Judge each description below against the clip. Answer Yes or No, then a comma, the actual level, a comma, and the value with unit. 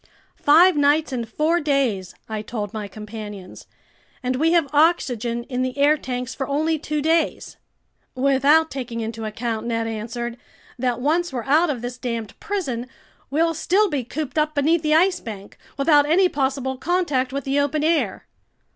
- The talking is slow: No, average, 165 wpm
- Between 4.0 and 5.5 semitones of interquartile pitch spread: Yes, average, 4.7 semitones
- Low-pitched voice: No, very high, 275 Hz